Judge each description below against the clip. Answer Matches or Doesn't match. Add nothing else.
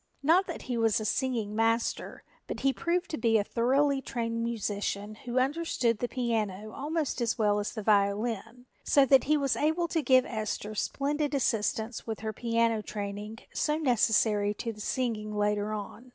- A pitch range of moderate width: Matches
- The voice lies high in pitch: Matches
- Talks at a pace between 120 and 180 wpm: Matches